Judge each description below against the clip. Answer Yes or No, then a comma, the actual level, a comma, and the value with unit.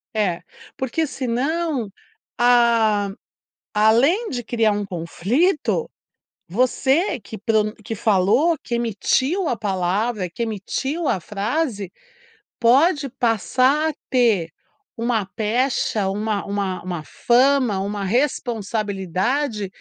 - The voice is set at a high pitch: Yes, high, 230 Hz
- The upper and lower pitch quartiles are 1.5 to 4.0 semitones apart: No, average, 4.7 semitones